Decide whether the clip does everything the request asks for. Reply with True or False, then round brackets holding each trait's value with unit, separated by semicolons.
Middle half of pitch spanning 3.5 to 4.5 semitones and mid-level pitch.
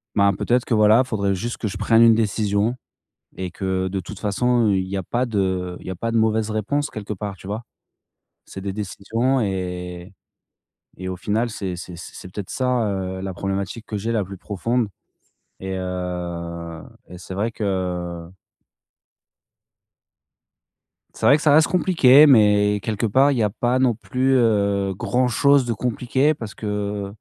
False (3.9 semitones; 105 Hz)